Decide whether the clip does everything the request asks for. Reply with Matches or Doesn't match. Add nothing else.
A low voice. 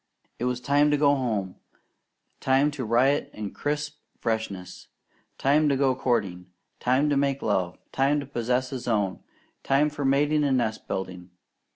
Matches